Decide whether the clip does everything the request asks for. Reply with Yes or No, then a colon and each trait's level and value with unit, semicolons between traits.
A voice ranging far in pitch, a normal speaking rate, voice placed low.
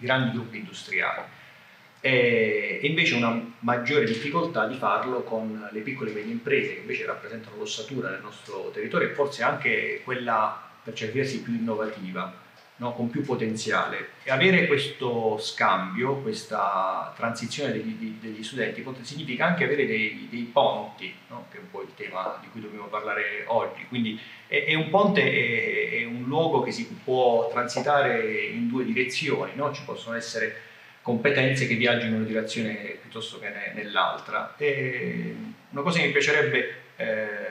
Yes: wide, 7.3 semitones; average, 160 wpm; low, 125 Hz